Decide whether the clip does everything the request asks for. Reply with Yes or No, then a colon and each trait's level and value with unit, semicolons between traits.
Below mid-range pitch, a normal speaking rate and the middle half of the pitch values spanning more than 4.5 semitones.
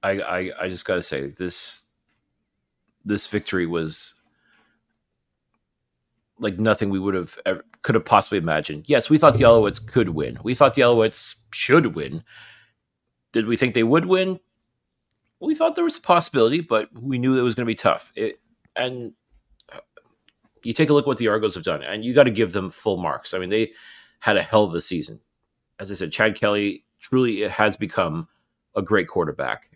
Yes: low, 115 Hz; average, 190 wpm; average, 5.0 semitones